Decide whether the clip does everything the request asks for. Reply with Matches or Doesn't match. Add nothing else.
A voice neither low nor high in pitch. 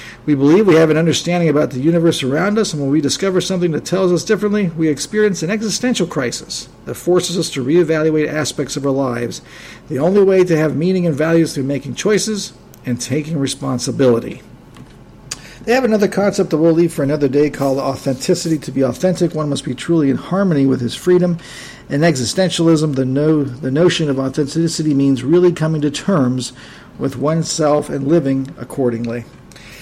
Matches